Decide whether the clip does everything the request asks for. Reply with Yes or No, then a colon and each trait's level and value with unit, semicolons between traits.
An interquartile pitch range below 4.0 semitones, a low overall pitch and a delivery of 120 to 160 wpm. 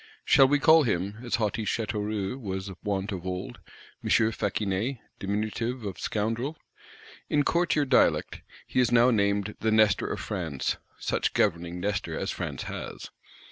Yes: average, 3.6 semitones; low, 105 Hz; average, 145 wpm